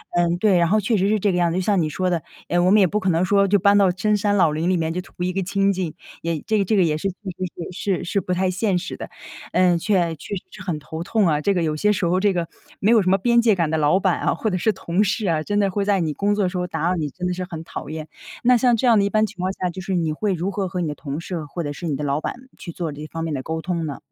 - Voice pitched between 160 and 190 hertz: Yes, medium, 185 Hz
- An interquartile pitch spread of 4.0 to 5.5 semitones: No, average, 3.3 semitones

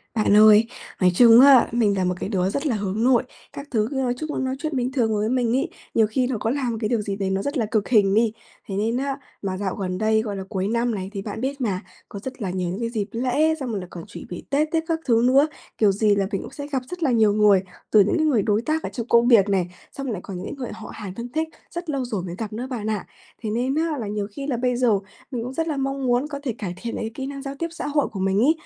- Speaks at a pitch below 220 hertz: No, high, 230 Hz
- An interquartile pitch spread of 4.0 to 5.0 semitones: Yes, average, 4.6 semitones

